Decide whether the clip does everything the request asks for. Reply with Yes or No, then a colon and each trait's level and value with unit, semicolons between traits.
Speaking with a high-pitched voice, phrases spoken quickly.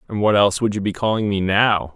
No: low, 100 Hz; fast, 275 wpm